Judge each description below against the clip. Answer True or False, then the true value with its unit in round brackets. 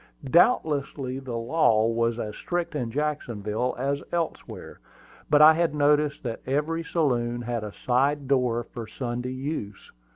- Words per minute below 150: True (140 wpm)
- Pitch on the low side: True (130 Hz)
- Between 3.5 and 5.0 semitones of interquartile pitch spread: True (4.0 semitones)